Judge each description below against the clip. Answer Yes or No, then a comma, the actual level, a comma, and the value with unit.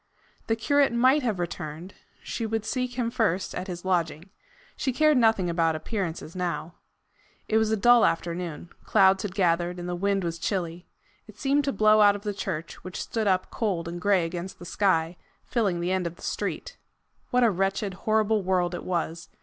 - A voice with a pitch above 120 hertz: Yes, high, 190 Hz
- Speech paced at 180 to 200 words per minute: Yes, average, 190 wpm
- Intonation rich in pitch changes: No, average, 4.1 semitones